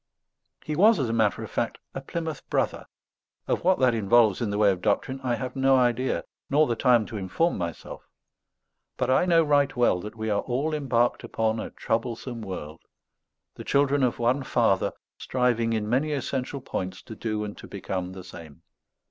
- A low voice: Yes, low, 120 Hz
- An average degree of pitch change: Yes, average, 4.2 semitones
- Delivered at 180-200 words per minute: Yes, average, 190 wpm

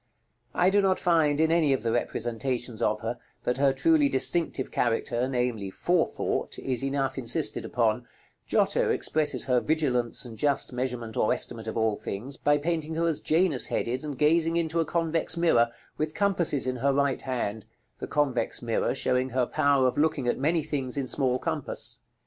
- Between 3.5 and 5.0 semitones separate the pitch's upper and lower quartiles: Yes, average, 4.5 semitones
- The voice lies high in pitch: No, low, 135 Hz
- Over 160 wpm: Yes, average, 180 wpm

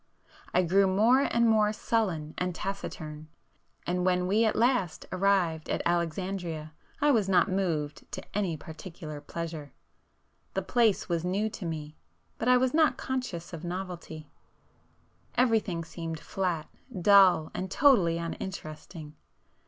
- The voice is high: No, medium, 180 Hz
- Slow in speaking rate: Yes, slow, 130 wpm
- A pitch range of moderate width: Yes, average, 4.1 semitones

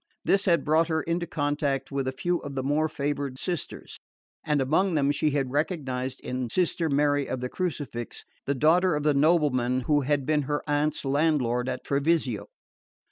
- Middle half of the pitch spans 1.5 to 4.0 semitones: Yes, average, 2.8 semitones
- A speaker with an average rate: Yes, average, 180 wpm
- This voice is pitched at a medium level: Yes, medium, 145 Hz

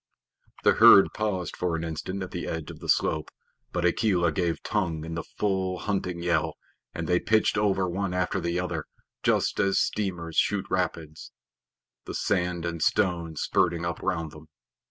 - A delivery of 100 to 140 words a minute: No, average, 170 wpm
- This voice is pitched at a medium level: No, very low, 90 Hz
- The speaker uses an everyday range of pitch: No, narrow, 2.2 semitones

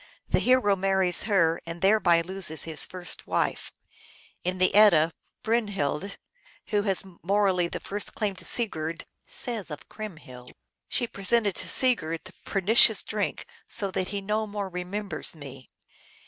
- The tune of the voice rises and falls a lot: No, average, 3.5 semitones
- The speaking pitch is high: Yes, high, 195 Hz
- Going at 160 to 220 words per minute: No, average, 145 wpm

